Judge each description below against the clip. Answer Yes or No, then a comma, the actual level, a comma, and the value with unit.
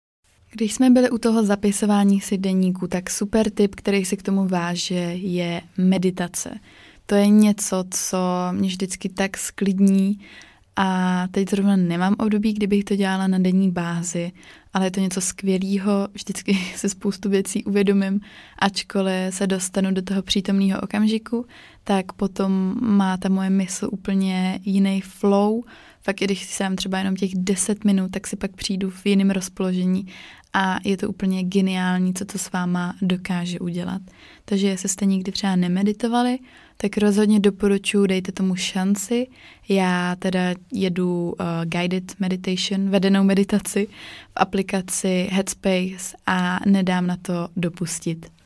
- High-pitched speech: Yes, high, 195 Hz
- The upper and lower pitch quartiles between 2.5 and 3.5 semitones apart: No, narrow, 1.5 semitones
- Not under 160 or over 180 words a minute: No, average, 145 wpm